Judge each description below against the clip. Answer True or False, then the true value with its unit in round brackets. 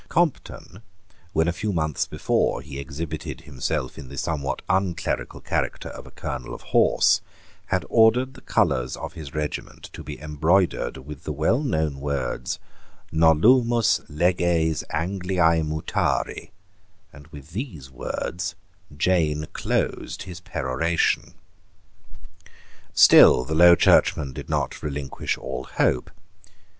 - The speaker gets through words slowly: True (125 wpm)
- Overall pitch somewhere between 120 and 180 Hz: False (80 Hz)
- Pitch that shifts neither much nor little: True (3.7 semitones)